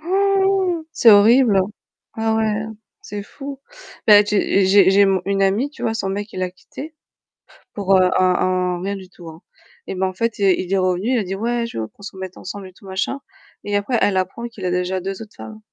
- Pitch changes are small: No, average, 3.3 semitones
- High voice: Yes, high, 200 Hz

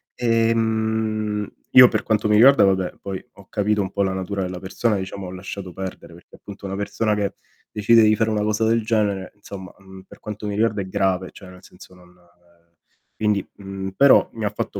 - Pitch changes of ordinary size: No, narrow, 2.3 semitones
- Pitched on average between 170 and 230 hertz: No, low, 100 Hz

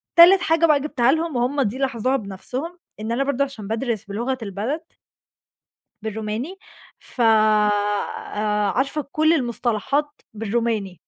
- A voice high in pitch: Yes, high, 240 Hz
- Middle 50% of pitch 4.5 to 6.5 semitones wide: Yes, average, 4.9 semitones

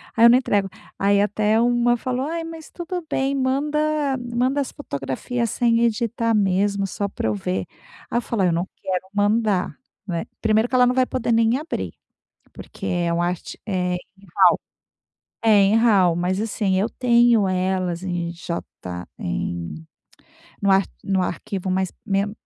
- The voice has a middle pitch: No, high, 205 Hz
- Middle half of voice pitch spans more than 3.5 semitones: Yes, average, 4.5 semitones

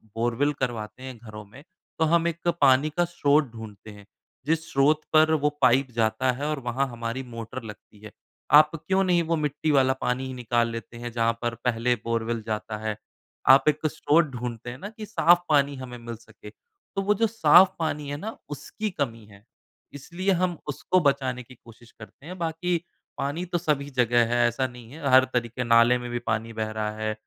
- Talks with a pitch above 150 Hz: No, low, 130 Hz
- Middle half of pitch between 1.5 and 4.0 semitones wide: No, average, 4.8 semitones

